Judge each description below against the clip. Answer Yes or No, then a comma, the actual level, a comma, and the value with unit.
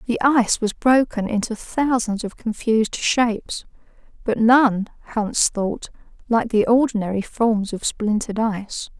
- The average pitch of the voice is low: No, high, 225 Hz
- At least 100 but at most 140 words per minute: Yes, slow, 135 wpm